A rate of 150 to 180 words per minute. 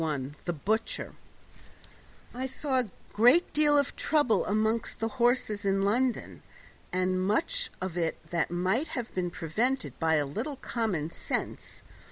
No: average, 140 wpm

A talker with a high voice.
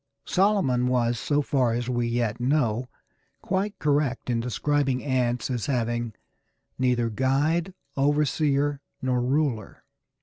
No: low, 130 Hz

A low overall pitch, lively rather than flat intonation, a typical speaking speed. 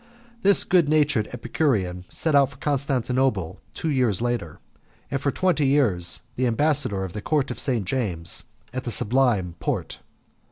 Yes: low, 130 Hz; wide, 5.9 semitones; average, 160 wpm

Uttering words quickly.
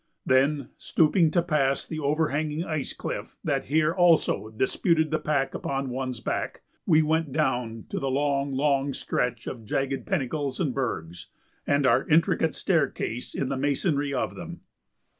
No: average, 155 wpm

